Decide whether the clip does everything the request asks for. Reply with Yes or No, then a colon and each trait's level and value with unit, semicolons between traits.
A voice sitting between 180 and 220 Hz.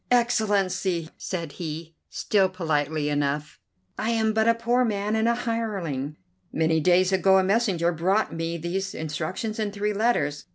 Yes: high, 190 Hz